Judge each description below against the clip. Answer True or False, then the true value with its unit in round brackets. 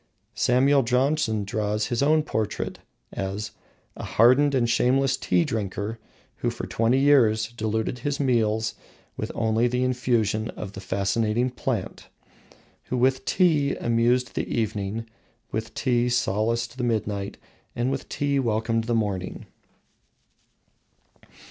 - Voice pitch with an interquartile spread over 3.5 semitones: False (2.9 semitones)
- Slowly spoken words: True (125 wpm)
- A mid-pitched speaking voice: False (115 Hz)